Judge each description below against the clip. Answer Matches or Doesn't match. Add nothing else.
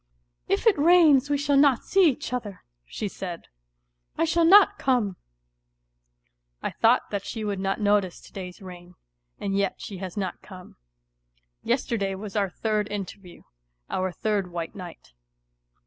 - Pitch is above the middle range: Matches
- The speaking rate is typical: Matches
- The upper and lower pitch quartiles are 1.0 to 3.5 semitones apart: Doesn't match